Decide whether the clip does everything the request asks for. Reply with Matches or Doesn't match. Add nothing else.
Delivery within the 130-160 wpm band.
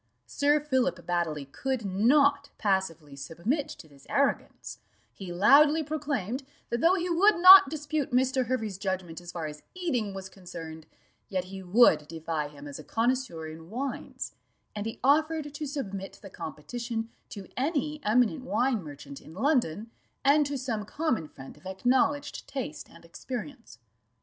Matches